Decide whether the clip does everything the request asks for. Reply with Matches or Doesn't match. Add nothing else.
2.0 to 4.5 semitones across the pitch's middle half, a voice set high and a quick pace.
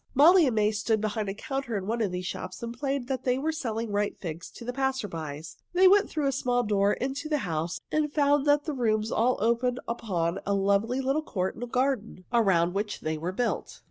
Doesn't match